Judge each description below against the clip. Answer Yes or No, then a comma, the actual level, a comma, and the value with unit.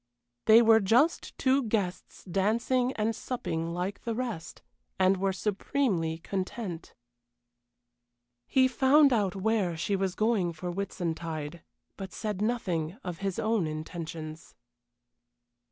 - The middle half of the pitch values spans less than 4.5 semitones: No, average, 4.8 semitones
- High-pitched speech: Yes, high, 195 Hz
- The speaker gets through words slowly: Yes, slow, 120 wpm